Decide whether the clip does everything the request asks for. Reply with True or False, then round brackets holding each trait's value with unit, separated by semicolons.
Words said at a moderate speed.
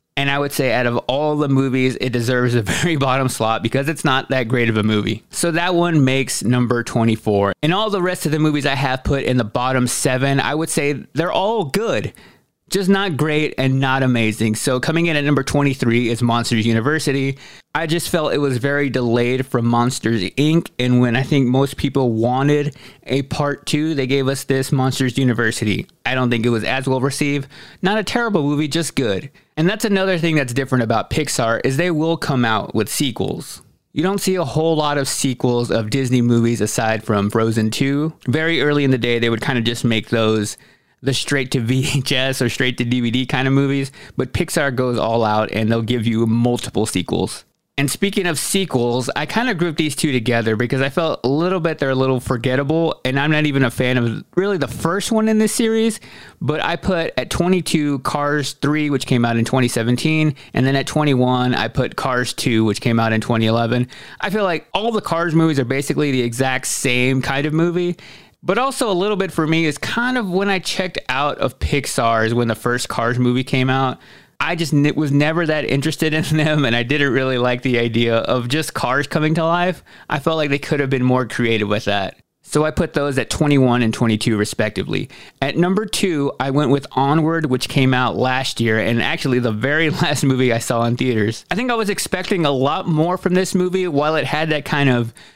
False (220 wpm)